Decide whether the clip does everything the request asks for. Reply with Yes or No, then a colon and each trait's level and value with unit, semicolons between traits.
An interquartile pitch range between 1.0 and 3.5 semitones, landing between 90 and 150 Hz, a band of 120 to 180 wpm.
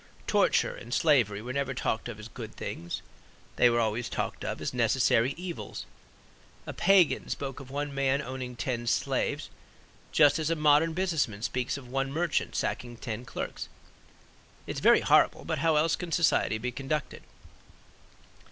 No: average, 4.1 semitones; low, 135 Hz; average, 160 wpm